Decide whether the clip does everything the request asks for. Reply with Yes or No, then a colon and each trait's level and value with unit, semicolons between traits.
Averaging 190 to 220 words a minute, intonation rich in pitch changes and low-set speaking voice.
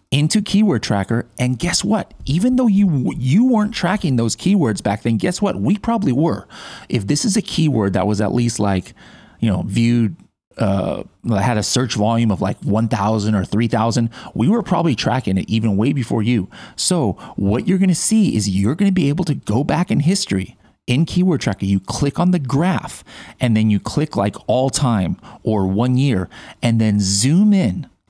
Yes: average, 195 wpm; wide, 8.8 semitones; low, 125 Hz